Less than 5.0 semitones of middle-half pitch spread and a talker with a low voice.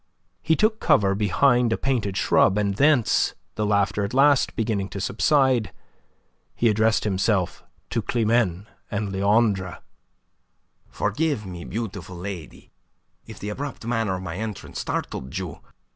Yes: average, 3.7 semitones; low, 105 Hz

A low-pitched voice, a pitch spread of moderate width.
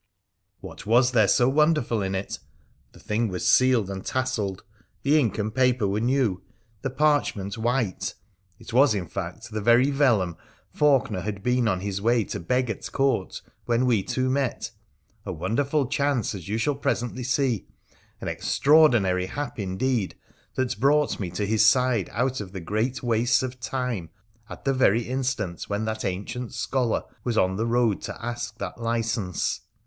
Yes: low, 115 Hz; average, 4.2 semitones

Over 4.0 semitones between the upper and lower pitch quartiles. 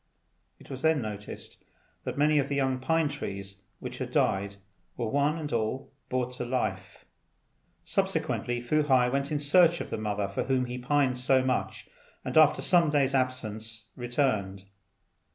Yes: average, 4.7 semitones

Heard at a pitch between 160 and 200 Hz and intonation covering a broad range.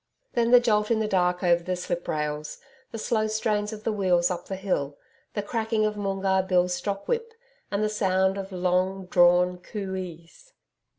No: high, 190 Hz; average, 3.0 semitones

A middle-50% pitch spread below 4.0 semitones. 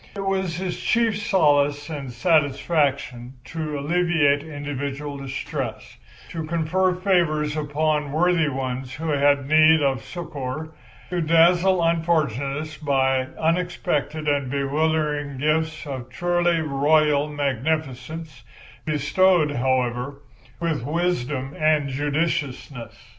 Yes: average, 2.9 semitones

